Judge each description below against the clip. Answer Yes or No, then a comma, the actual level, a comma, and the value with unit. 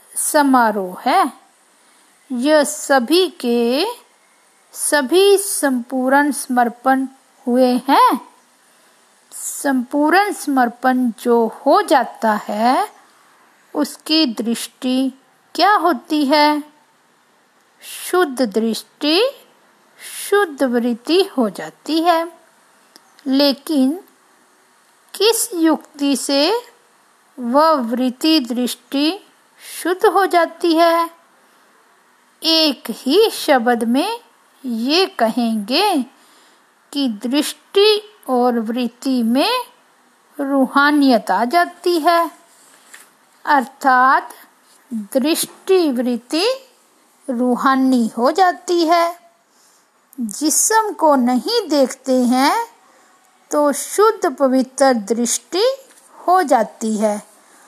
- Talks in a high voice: Yes, very high, 285 Hz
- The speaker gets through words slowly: Yes, slow, 75 wpm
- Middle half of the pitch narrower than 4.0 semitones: No, wide, 5.5 semitones